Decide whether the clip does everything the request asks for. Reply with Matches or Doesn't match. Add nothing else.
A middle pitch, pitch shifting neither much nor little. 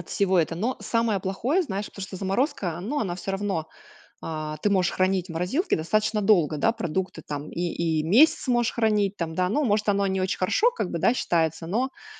Doesn't match